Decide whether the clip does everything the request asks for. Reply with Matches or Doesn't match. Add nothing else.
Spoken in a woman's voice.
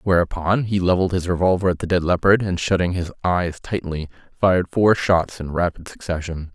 Doesn't match